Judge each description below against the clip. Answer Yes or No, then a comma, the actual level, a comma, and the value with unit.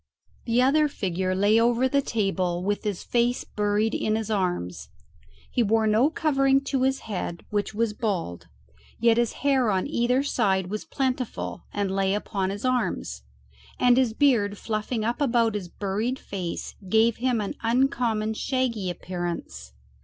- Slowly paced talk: No, average, 155 wpm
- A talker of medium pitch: No, high, 220 Hz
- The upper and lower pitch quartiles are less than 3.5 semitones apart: No, average, 4.1 semitones